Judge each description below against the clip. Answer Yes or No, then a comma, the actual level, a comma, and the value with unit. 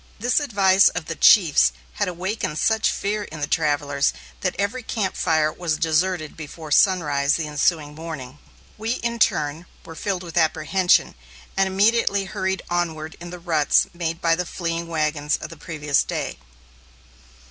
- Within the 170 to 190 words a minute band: No, average, 160 wpm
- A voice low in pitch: No, medium, 170 Hz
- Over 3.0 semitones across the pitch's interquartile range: Yes, average, 3.7 semitones